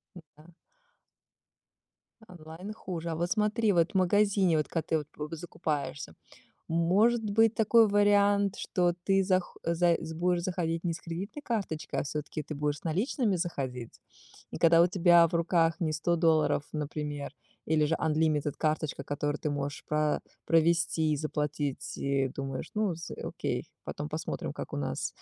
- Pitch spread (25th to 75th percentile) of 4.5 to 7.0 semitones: No, average, 3.6 semitones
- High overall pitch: No, medium, 165 Hz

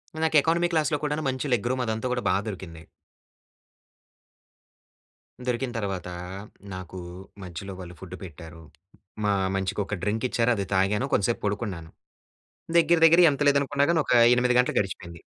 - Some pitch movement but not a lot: No, wide, 6.9 semitones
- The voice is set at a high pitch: No, low, 110 Hz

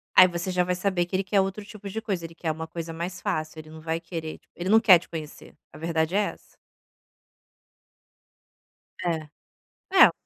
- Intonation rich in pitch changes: No, average, 2.7 semitones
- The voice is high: No, medium, 175 Hz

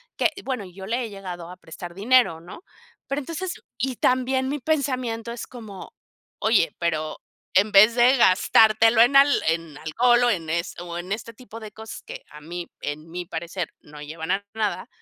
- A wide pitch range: Yes, wide, 6.2 semitones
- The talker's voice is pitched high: Yes, high, 210 Hz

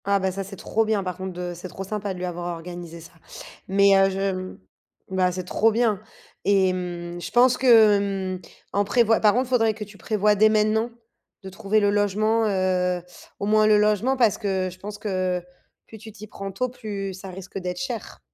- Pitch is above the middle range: Yes, high, 200 Hz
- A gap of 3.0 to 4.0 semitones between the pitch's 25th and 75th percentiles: No, narrow, 2.6 semitones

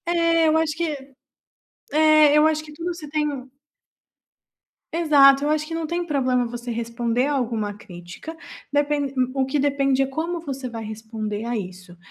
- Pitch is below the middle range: No, very high, 280 Hz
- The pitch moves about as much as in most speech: Yes, average, 4.8 semitones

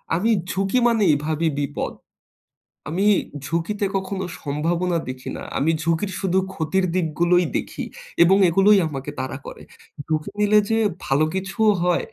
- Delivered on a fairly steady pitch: No, average, 3.7 semitones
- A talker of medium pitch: Yes, medium, 175 Hz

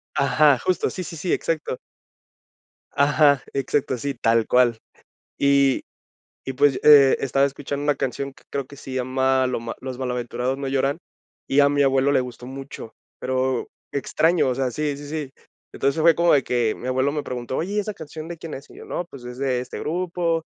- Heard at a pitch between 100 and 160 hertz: Yes, low, 135 Hz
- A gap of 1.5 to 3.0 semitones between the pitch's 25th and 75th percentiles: Yes, narrow, 2.5 semitones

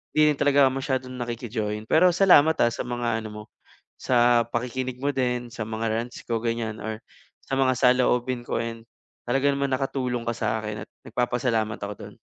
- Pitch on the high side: No, low, 120 Hz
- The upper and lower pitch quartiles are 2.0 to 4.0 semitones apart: Yes, narrow, 2.4 semitones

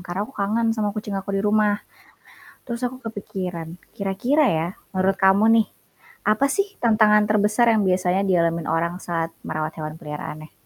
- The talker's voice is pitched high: Yes, high, 200 Hz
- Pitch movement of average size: Yes, average, 3.9 semitones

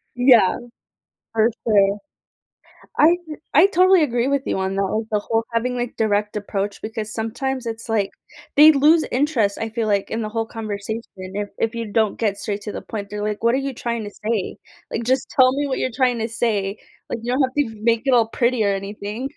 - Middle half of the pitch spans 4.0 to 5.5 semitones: No, average, 3.3 semitones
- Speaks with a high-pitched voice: Yes, high, 225 Hz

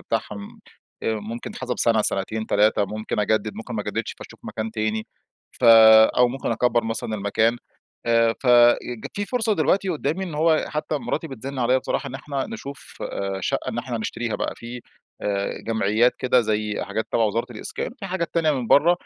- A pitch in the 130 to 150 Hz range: No, low, 120 Hz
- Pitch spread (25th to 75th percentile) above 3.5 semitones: Yes, average, 4.1 semitones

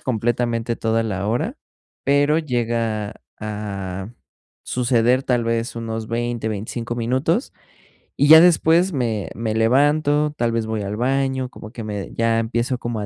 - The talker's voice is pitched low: Yes, low, 115 Hz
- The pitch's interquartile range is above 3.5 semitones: No, average, 2.8 semitones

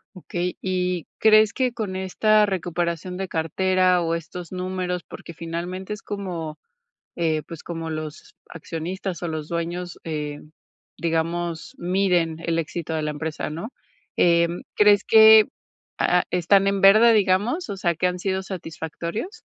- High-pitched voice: No, medium, 180 Hz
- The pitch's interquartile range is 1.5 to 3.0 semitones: Yes, narrow, 2.6 semitones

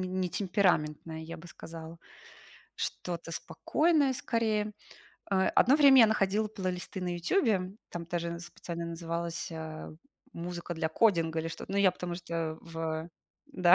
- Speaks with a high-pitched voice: No, medium, 175 Hz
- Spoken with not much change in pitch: No, average, 3.2 semitones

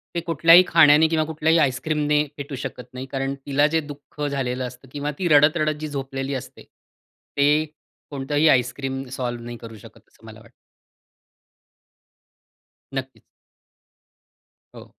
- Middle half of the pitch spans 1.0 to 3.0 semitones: Yes, narrow, 2.4 semitones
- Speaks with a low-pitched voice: No, medium, 145 Hz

